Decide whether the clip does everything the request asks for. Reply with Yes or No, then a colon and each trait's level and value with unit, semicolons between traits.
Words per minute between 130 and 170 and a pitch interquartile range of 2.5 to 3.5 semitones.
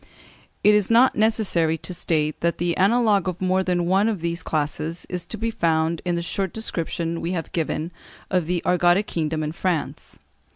No: average, 190 wpm; average, 2.8 semitones